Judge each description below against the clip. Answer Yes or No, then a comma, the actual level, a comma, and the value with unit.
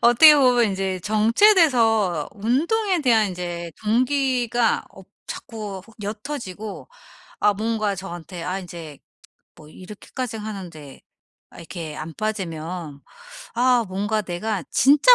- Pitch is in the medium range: No, high, 210 Hz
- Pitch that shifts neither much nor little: Yes, average, 5.0 semitones